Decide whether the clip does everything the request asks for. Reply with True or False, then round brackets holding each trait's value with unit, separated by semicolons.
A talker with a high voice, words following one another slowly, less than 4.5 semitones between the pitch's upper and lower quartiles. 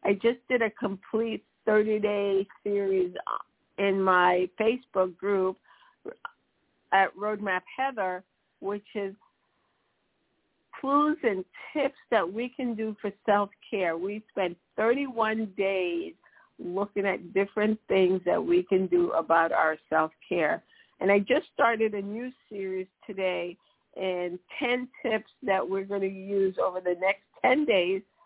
True (200 Hz; 130 wpm; 3.0 semitones)